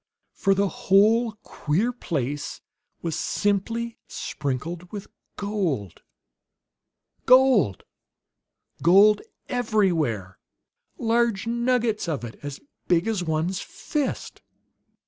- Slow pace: Yes, slow, 90 wpm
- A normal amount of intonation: No, wide, 6.4 semitones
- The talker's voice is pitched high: Yes, high, 195 Hz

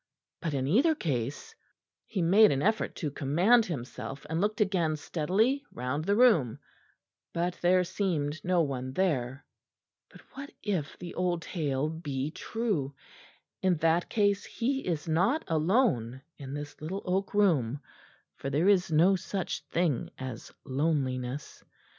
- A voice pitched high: No, medium, 165 Hz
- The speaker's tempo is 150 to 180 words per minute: No, average, 140 wpm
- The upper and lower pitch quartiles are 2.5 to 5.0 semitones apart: No, wide, 5.6 semitones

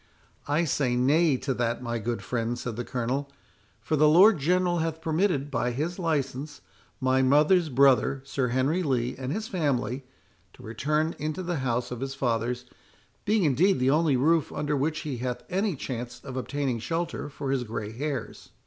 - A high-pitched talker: No, medium, 140 Hz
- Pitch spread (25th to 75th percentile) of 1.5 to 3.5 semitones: No, average, 4.1 semitones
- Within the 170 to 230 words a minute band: Yes, average, 175 wpm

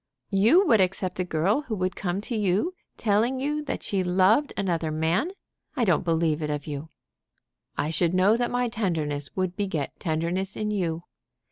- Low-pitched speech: No, medium, 185 Hz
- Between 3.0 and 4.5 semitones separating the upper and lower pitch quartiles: No, average, 4.9 semitones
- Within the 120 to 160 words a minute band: No, average, 175 wpm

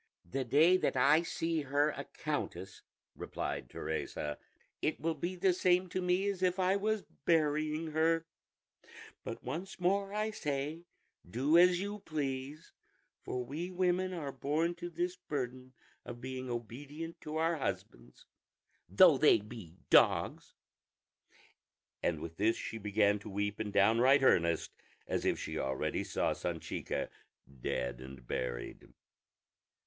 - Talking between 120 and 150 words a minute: Yes, average, 140 wpm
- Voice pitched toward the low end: No, medium, 150 Hz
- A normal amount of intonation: No, wide, 6.9 semitones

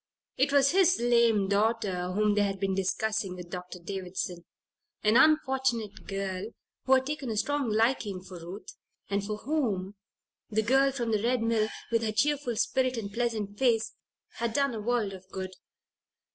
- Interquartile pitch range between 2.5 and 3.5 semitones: No, average, 4.2 semitones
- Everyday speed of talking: Yes, average, 170 wpm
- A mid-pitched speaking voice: No, high, 220 Hz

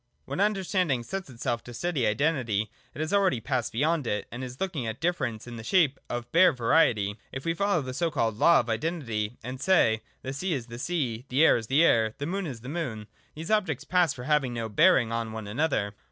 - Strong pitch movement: Yes, wide, 6.3 semitones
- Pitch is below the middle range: Yes, low, 130 Hz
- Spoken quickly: Yes, fast, 225 wpm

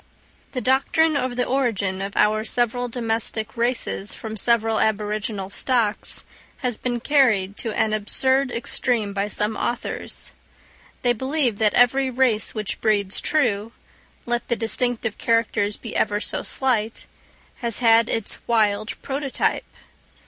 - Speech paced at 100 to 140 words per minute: Yes, slow, 135 wpm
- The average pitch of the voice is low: No, high, 230 Hz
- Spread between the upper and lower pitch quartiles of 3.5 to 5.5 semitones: No, average, 2.8 semitones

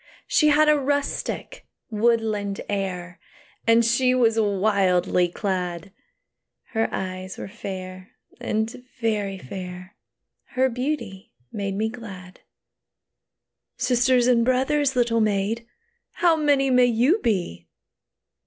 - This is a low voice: No, high, 220 Hz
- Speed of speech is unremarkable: No, slow, 105 wpm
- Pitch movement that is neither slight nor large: Yes, average, 4.8 semitones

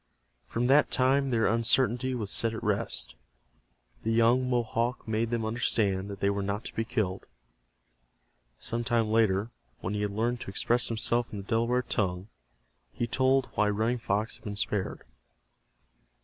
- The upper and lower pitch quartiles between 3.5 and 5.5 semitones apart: No, average, 2.7 semitones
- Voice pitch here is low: Yes, low, 115 Hz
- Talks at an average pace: Yes, average, 165 wpm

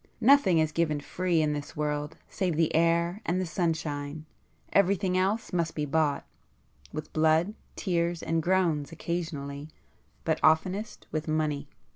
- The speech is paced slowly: Yes, slow, 125 wpm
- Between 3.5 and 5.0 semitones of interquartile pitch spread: No, average, 2.8 semitones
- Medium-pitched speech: Yes, medium, 160 Hz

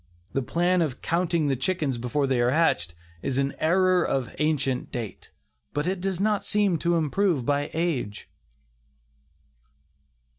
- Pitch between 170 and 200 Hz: No, medium, 155 Hz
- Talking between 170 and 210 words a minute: No, average, 145 wpm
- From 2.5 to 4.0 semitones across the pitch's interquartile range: No, average, 5.0 semitones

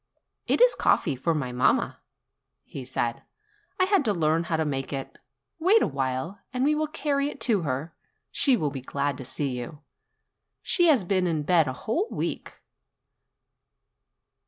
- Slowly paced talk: No, average, 165 wpm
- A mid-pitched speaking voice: Yes, medium, 160 Hz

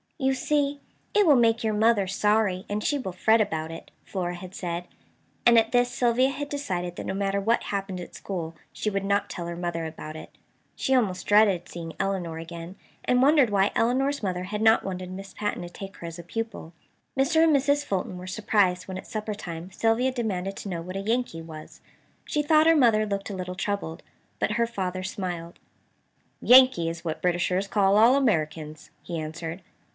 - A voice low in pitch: No, high, 195 Hz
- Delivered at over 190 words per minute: Yes, average, 200 wpm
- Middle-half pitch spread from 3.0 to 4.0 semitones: No, average, 4.6 semitones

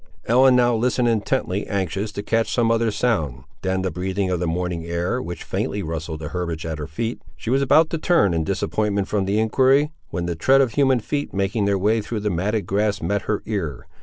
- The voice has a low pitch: Yes, low, 100 Hz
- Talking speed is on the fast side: Yes, fast, 220 wpm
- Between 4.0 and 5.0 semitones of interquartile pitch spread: Yes, average, 4.7 semitones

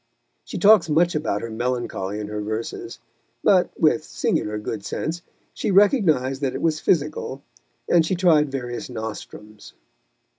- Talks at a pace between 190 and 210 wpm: No, average, 145 wpm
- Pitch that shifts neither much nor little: No, wide, 6.9 semitones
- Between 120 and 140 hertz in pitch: Yes, low, 135 Hz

